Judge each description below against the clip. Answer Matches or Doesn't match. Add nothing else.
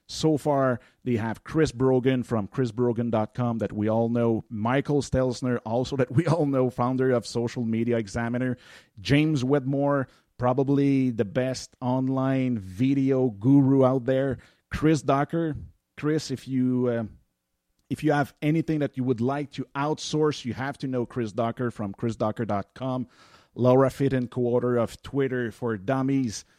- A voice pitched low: Matches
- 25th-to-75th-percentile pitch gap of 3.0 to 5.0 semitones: Doesn't match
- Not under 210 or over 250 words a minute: Doesn't match